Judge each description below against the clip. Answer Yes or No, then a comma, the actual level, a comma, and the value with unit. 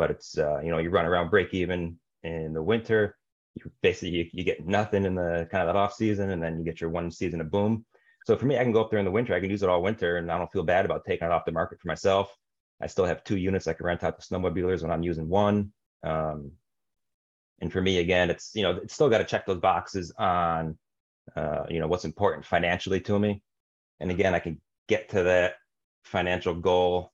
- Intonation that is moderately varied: Yes, average, 3.0 semitones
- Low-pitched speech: Yes, very low, 90 Hz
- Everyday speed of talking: No, fast, 250 wpm